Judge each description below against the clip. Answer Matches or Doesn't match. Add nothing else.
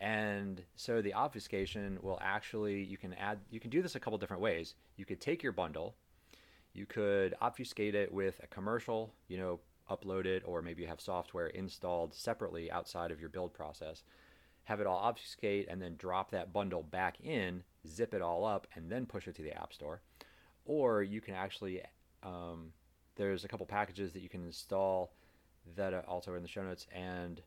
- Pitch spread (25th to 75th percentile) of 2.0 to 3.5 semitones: Matches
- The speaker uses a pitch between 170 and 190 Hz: Doesn't match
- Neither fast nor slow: Matches